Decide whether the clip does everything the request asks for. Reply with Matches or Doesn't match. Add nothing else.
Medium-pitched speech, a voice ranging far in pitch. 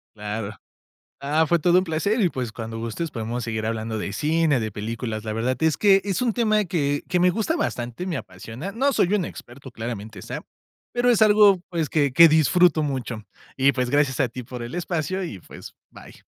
Matches